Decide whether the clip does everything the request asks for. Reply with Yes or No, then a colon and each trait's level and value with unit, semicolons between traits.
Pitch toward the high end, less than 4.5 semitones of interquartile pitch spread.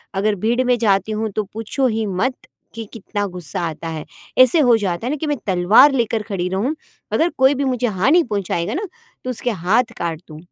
No: high, 220 Hz; average, 5.1 semitones